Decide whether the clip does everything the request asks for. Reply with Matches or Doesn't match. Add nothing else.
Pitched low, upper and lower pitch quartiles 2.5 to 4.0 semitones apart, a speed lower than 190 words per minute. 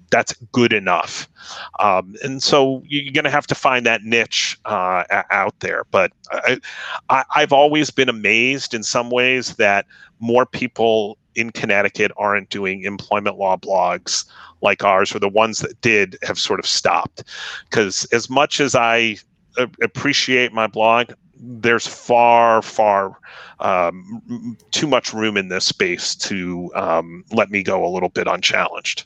Matches